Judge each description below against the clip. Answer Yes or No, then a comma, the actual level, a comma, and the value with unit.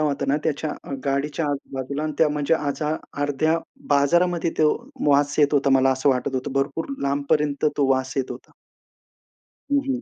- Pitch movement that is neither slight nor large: No, narrow, 2.0 semitones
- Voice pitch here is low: No, medium, 145 Hz